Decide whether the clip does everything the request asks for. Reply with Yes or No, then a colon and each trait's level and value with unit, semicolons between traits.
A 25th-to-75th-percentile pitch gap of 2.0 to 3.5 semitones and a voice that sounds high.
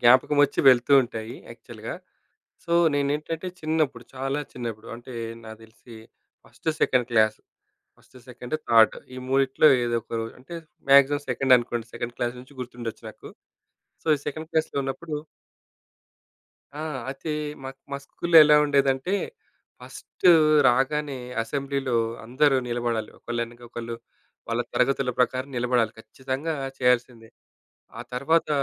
No: average, 3.0 semitones; low, 130 Hz